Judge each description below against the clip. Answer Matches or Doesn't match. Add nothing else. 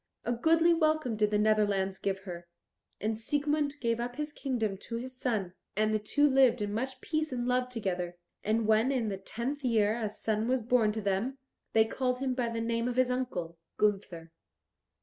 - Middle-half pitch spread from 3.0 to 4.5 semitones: Matches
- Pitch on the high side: Matches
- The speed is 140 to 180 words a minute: Doesn't match